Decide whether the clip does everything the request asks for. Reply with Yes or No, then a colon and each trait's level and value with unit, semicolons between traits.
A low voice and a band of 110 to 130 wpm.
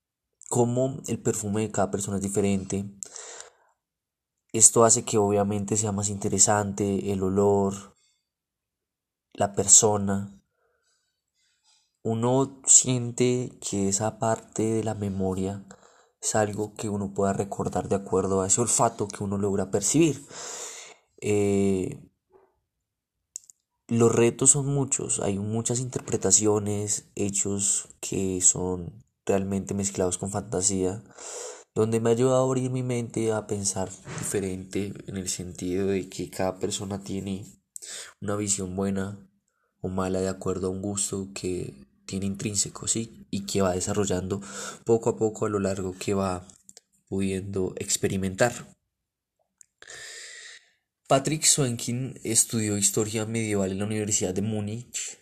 Yes: low, 100 Hz; slow, 125 wpm